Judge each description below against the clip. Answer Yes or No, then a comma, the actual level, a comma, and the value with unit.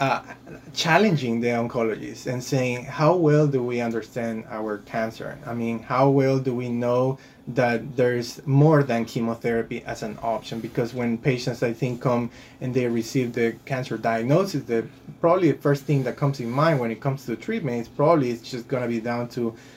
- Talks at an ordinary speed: Yes, average, 190 wpm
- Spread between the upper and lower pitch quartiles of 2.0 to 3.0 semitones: Yes, narrow, 2.5 semitones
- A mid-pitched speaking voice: No, low, 125 Hz